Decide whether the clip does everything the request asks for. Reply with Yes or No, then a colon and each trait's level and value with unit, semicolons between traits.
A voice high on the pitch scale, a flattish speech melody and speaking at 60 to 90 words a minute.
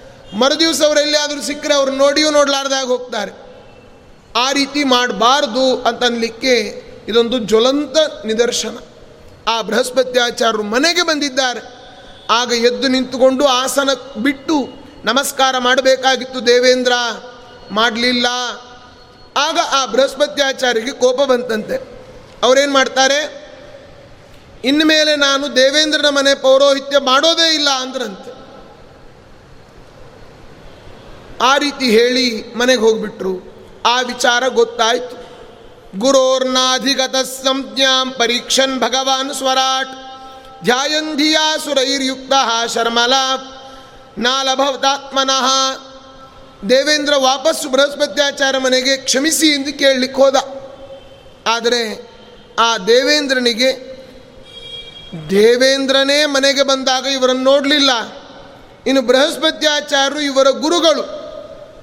Yes: very high, 265 Hz; narrow, 2.2 semitones; average, 80 wpm